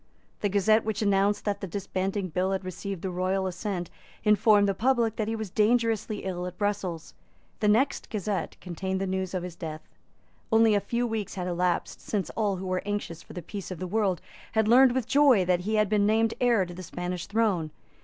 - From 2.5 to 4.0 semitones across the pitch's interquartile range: Yes, average, 3.0 semitones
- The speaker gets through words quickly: Yes, fast, 210 wpm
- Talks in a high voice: Yes, high, 200 Hz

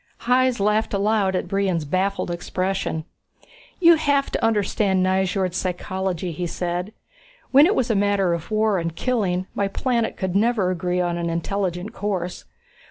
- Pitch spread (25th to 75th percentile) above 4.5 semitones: No, average, 3.1 semitones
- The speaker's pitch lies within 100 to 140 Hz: No, high, 190 Hz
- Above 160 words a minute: No, average, 155 wpm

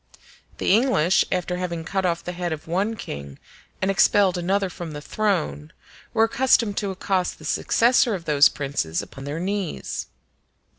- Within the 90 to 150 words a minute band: No, average, 160 wpm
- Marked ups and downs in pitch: No, average, 4.3 semitones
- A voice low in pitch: No, medium, 180 Hz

